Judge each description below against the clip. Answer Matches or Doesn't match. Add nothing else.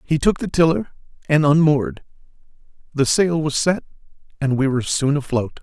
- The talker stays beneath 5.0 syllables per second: Doesn't match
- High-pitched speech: Doesn't match